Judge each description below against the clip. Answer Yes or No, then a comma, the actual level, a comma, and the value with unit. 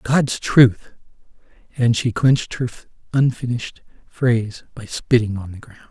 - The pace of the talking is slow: Yes, slow, 130 wpm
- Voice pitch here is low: Yes, low, 120 Hz